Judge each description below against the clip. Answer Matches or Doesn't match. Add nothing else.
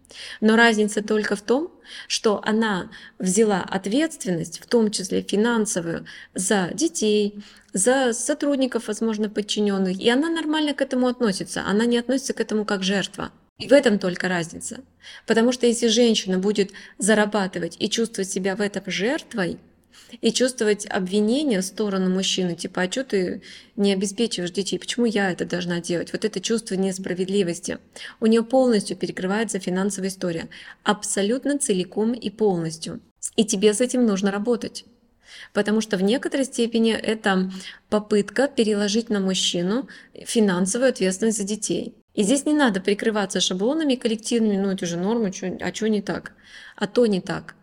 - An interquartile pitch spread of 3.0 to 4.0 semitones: Matches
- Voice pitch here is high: Matches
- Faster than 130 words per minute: Matches